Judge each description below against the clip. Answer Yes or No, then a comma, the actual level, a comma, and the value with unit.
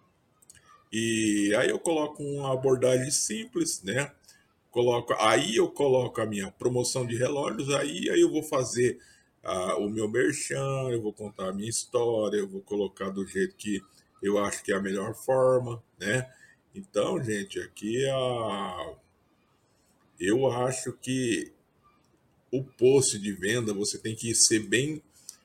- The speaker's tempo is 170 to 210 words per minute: No, average, 150 wpm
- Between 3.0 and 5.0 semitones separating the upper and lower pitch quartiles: Yes, average, 4.0 semitones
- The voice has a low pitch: Yes, low, 125 Hz